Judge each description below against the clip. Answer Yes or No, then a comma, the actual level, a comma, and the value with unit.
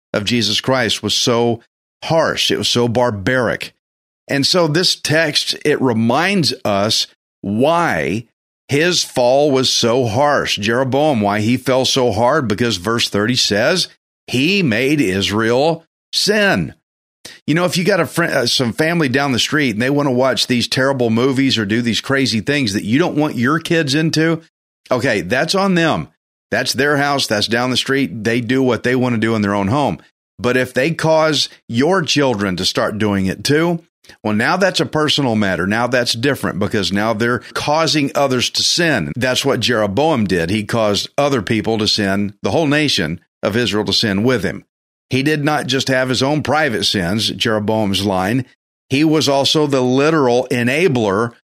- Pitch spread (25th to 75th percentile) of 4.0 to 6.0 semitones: Yes, average, 4.9 semitones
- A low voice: Yes, low, 125 Hz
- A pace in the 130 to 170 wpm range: No, average, 180 wpm